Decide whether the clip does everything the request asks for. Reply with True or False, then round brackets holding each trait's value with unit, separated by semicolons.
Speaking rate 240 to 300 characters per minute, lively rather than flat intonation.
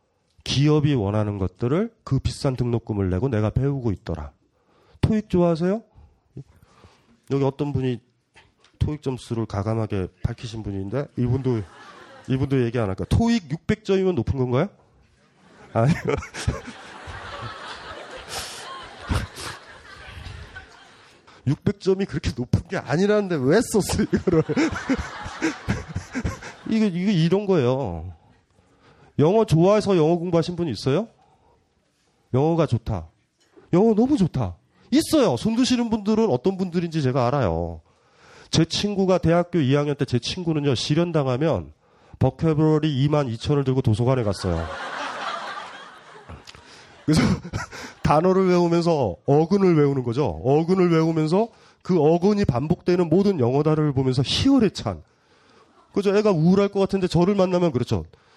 True (265 characters per minute; 7.3 semitones)